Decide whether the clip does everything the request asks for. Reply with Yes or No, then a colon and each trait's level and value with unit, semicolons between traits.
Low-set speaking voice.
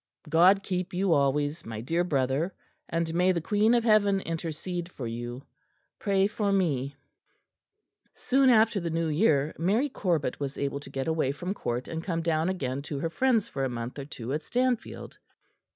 No: medium, 165 Hz